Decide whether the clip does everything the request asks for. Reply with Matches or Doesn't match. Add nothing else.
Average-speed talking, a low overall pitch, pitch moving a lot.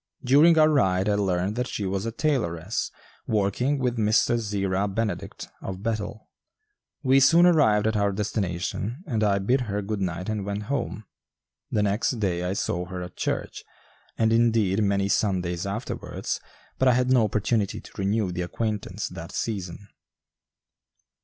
Doesn't match